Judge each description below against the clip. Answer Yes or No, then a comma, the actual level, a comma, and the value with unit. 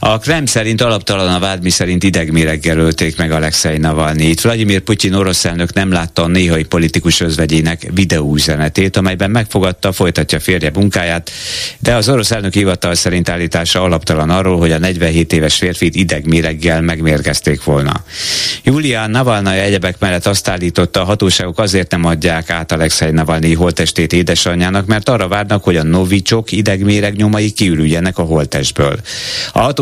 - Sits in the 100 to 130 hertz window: No, very low, 90 Hz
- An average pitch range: Yes, average, 3.3 semitones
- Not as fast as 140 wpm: No, average, 150 wpm